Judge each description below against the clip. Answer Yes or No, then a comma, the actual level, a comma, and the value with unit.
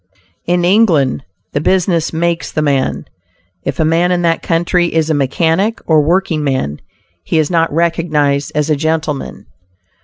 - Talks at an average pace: Yes, average, 155 wpm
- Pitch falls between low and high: Yes, medium, 160 Hz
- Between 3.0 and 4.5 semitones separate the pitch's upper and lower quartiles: No, narrow, 2.5 semitones